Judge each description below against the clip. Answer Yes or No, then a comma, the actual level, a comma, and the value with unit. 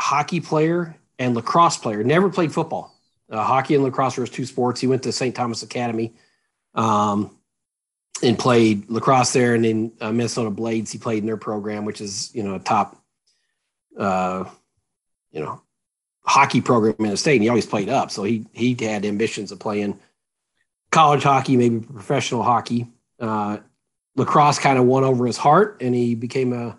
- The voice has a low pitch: Yes, low, 120 Hz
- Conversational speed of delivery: Yes, average, 180 wpm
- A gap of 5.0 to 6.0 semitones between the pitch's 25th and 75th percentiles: No, average, 3.2 semitones